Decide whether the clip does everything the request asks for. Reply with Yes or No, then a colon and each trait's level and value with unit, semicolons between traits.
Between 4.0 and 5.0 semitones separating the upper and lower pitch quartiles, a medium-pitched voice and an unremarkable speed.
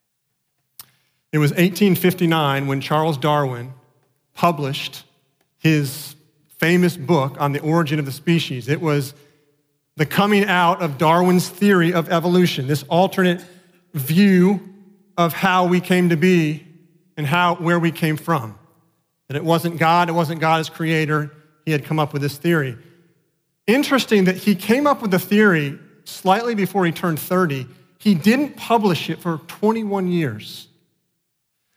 No: average, 3.2 semitones; medium, 165 Hz; average, 145 wpm